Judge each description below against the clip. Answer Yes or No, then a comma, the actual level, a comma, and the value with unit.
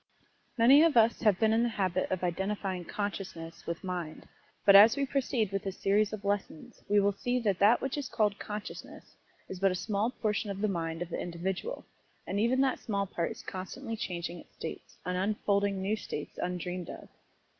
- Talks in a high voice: Yes, high, 200 Hz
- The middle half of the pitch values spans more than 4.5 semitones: No, average, 3.3 semitones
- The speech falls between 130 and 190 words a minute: No, average, 200 wpm